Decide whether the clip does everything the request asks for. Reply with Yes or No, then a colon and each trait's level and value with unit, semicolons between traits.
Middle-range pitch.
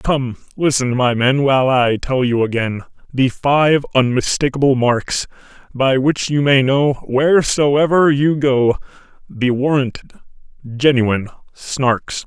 No: low, 130 Hz